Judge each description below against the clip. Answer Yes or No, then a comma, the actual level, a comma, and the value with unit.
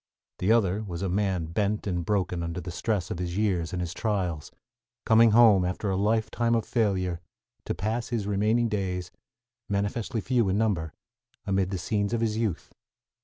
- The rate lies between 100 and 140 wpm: No, average, 175 wpm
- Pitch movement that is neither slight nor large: Yes, average, 3.4 semitones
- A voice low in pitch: Yes, low, 100 Hz